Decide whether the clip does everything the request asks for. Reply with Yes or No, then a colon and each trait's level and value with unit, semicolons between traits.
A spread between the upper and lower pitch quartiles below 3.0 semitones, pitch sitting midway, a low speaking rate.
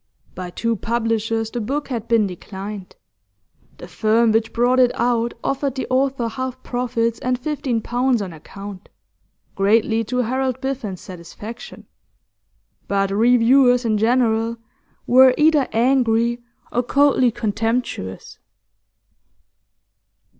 No: narrow, 2.6 semitones; high, 235 Hz; slow, 115 wpm